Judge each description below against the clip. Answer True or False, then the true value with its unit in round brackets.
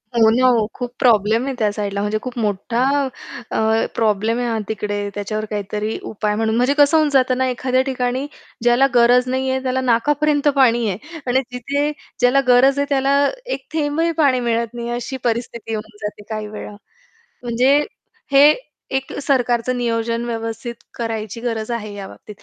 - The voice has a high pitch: True (240 Hz)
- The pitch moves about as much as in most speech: True (3.0 semitones)